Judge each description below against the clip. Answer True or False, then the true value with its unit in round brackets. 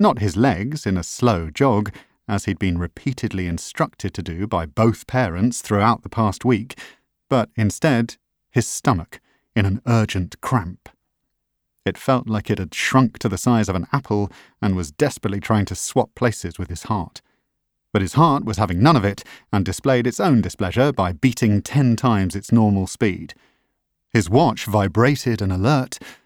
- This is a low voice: True (110 Hz)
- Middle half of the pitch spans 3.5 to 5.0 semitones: True (4.1 semitones)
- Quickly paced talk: False (175 wpm)